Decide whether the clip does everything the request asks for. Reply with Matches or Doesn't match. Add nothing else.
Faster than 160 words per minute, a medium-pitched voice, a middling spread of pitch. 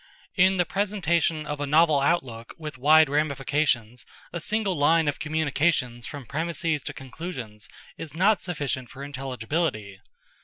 Doesn't match